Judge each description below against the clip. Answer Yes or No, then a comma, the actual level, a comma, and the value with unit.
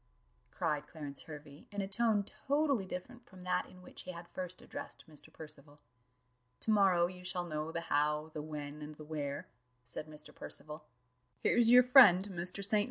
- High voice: No, medium, 170 Hz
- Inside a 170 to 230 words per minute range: Yes, average, 175 wpm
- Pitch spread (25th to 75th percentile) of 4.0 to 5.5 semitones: Yes, average, 4.3 semitones